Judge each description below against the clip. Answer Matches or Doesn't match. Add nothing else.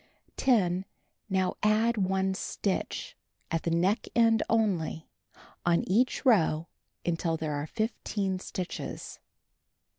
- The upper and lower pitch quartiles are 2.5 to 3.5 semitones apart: Doesn't match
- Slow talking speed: Matches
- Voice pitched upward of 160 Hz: Matches